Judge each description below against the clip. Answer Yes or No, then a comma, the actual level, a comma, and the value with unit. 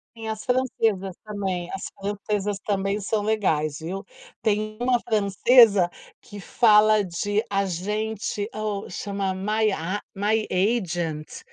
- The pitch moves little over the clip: Yes, narrow, 2.1 semitones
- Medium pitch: No, high, 205 Hz